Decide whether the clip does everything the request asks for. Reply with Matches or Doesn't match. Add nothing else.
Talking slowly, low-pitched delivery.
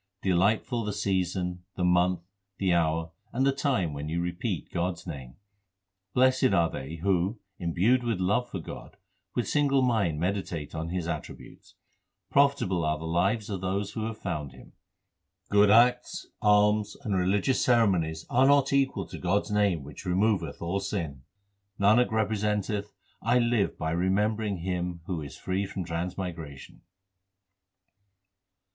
Doesn't match